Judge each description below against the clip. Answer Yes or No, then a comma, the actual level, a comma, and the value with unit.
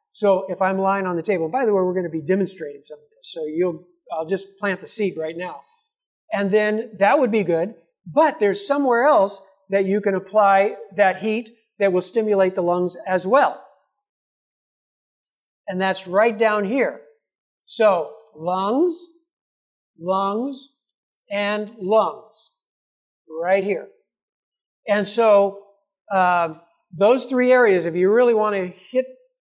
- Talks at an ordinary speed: Yes, average, 150 wpm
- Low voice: No, high, 200 Hz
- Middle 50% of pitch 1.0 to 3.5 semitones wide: No, average, 4.3 semitones